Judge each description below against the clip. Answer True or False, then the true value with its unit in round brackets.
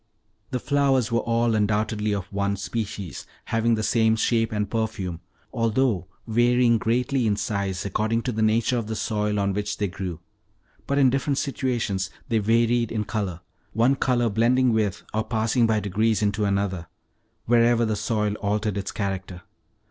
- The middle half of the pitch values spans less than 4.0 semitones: True (2.5 semitones)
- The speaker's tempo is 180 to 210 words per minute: False (165 wpm)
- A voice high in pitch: False (110 Hz)